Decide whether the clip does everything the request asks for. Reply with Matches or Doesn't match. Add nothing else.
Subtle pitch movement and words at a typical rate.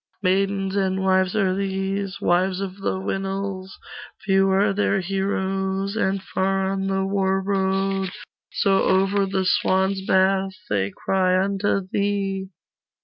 Doesn't match